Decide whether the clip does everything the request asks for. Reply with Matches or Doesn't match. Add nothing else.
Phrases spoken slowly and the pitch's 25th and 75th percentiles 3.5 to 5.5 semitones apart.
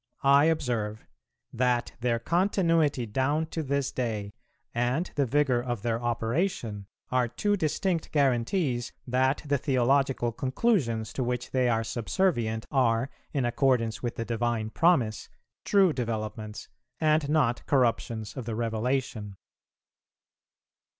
Matches